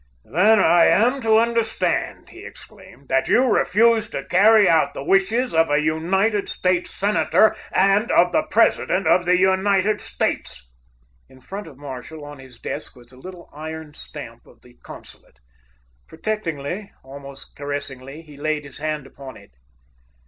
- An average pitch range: No, wide, 6.2 semitones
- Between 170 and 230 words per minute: No, average, 155 wpm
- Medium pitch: Yes, medium, 165 Hz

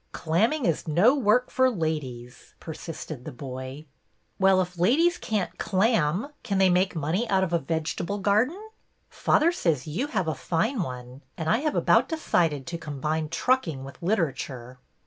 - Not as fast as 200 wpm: Yes, average, 165 wpm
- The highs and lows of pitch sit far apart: Yes, wide, 6.5 semitones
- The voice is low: No, medium, 170 Hz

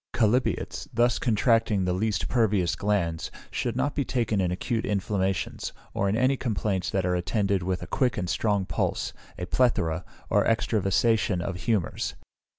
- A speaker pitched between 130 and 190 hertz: No, low, 105 Hz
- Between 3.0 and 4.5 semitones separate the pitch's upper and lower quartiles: Yes, average, 3.8 semitones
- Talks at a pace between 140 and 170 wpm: Yes, average, 155 wpm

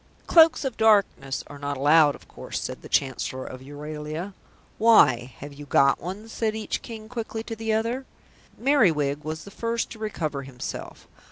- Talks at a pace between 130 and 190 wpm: Yes, average, 170 wpm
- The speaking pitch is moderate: Yes, medium, 170 Hz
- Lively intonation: Yes, wide, 7.7 semitones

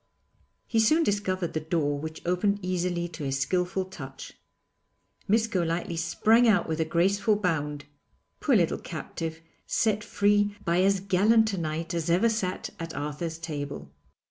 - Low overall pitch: No, medium, 175 Hz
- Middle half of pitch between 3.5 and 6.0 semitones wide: Yes, average, 4.1 semitones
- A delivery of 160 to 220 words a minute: No, average, 150 wpm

